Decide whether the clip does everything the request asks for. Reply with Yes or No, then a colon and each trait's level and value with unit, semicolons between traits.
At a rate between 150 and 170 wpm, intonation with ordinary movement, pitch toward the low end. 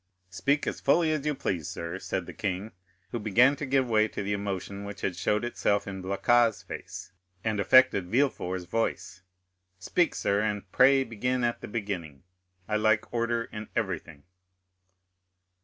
Yes: average, 160 wpm; average, 3.8 semitones; low, 105 Hz